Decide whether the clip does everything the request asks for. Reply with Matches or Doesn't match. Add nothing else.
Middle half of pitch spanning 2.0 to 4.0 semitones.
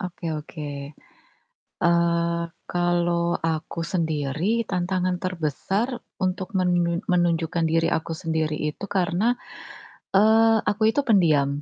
Matches